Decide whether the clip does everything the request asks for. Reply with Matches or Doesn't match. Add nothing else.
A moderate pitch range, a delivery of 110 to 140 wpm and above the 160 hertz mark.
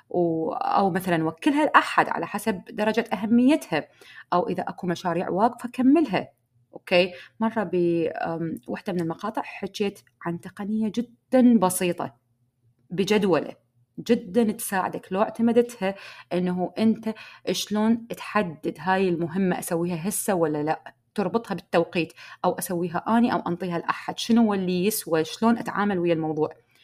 Matches